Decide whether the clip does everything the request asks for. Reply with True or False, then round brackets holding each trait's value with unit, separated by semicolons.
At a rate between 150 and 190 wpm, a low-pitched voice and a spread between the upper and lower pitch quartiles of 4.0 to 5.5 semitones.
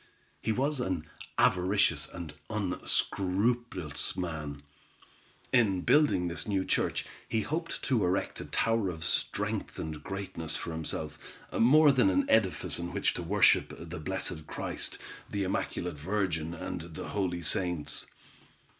False (135 wpm; 95 Hz; 4.6 semitones)